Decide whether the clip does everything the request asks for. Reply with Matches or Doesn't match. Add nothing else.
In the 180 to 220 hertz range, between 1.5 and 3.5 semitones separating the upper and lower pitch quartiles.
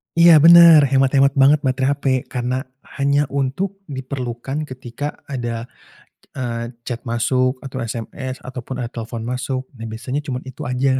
Doesn't match